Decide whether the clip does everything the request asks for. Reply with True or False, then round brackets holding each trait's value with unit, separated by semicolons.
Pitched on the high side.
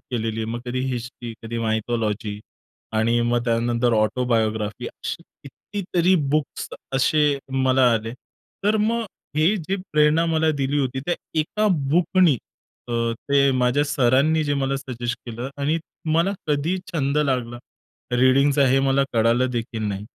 False (130 Hz)